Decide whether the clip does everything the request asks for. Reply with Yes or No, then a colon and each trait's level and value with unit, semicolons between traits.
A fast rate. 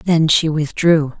No: average, 150 wpm